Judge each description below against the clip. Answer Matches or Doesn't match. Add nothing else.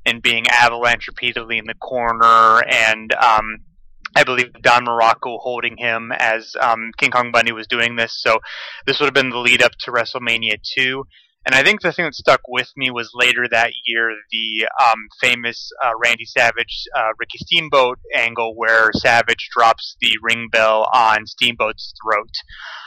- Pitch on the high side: Doesn't match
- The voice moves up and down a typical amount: Doesn't match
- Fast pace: Doesn't match